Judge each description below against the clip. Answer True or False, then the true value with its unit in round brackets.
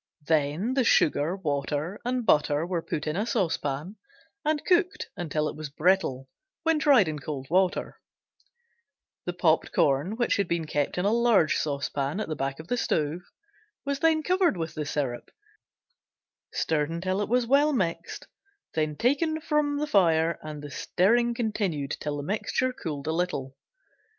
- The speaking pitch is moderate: True (175 Hz)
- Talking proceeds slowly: False (160 wpm)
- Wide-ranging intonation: True (8.0 semitones)